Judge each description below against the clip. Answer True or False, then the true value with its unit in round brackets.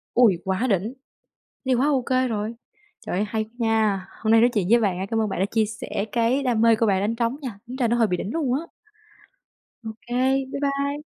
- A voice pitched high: True (230 Hz)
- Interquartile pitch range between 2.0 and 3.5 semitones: True (3.2 semitones)